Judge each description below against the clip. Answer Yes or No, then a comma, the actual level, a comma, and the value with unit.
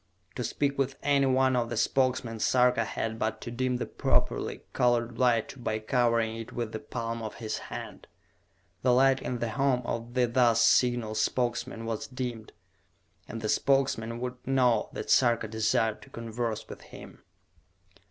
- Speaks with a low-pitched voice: Yes, low, 120 Hz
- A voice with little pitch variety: Yes, narrow, 2.0 semitones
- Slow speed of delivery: No, average, 165 wpm